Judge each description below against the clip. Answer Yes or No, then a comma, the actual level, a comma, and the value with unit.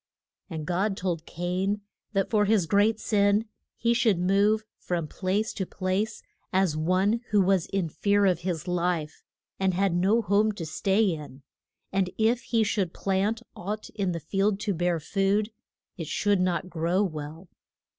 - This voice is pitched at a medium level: No, high, 195 Hz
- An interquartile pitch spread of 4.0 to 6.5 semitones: No, average, 2.8 semitones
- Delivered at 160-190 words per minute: Yes, average, 165 wpm